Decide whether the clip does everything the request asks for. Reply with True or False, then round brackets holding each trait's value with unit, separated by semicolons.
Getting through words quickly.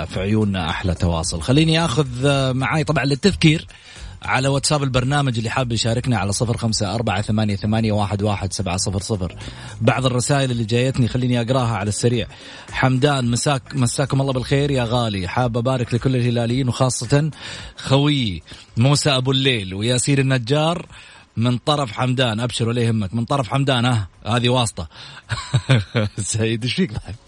True (140 wpm)